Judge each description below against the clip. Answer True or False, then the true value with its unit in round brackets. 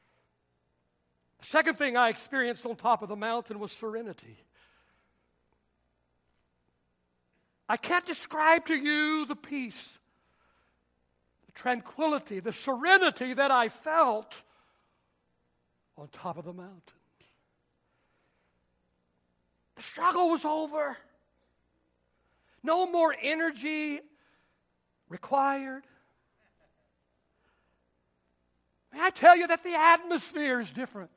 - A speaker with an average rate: False (90 wpm)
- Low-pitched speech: False (190 Hz)